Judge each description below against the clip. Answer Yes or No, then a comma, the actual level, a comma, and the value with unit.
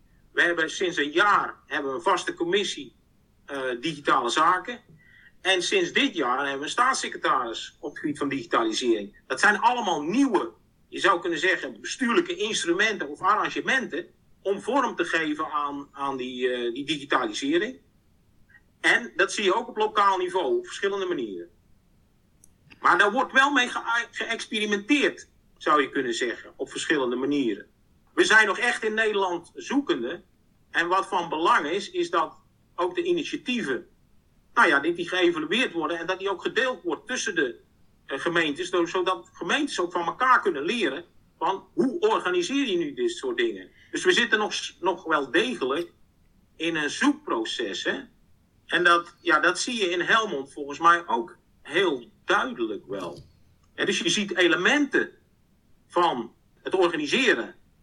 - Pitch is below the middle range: No, very high, 265 Hz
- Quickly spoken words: No, average, 160 wpm